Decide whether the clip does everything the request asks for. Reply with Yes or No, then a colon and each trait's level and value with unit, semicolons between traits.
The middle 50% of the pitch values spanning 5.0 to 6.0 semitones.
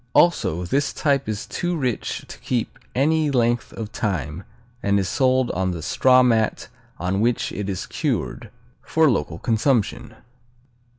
Yes: wide, 5.4 semitones